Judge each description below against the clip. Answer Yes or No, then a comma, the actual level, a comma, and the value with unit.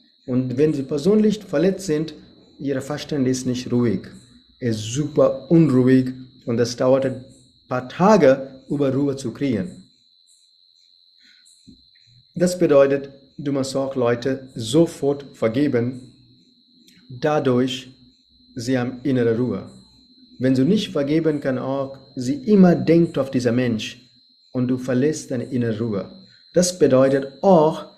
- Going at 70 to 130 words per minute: Yes, slow, 125 wpm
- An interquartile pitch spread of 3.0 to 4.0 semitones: Yes, average, 3.3 semitones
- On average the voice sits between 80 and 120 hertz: No, low, 135 Hz